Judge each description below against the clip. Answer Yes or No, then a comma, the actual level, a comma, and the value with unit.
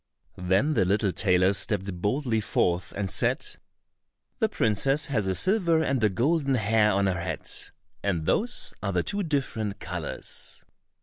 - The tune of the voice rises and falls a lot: Yes, wide, 6.4 semitones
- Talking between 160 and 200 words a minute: No, average, 150 wpm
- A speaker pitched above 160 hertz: No, low, 105 Hz